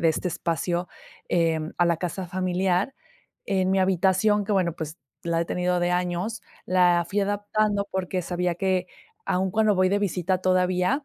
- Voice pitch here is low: No, medium, 185 Hz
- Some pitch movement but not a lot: No, narrow, 1.7 semitones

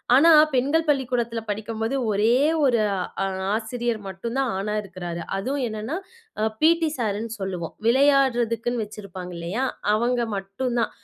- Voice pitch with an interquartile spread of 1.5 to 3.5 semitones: No, average, 3.9 semitones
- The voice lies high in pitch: Yes, high, 230 Hz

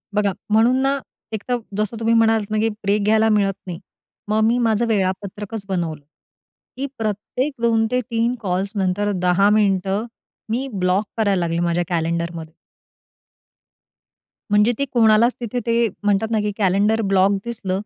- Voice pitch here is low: No, high, 210 Hz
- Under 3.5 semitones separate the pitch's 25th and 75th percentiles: Yes, average, 2.8 semitones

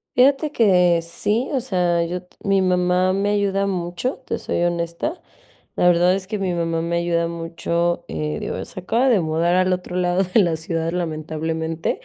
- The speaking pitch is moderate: Yes, medium, 180 Hz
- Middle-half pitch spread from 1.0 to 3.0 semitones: Yes, narrow, 2.5 semitones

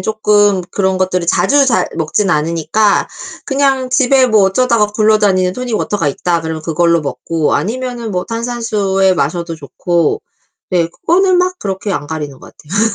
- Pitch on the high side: Yes, high, 195 Hz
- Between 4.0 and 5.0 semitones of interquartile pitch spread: No, wide, 5.5 semitones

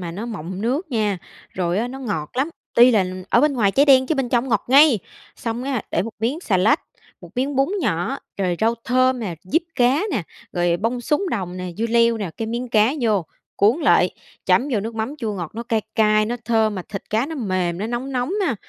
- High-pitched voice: Yes, high, 230 Hz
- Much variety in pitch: No, average, 4.4 semitones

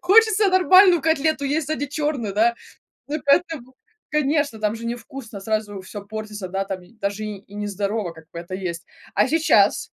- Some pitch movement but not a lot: No, wide, 7.0 semitones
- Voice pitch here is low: No, high, 230 Hz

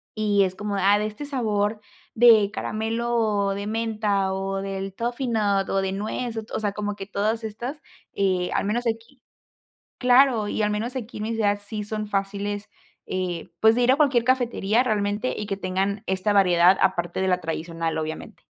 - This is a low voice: No, high, 210 Hz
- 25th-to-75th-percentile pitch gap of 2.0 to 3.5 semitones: Yes, narrow, 2.6 semitones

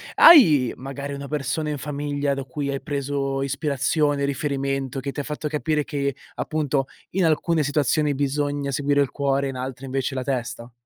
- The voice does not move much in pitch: Yes, narrow, 1.4 semitones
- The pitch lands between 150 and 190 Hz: No, medium, 140 Hz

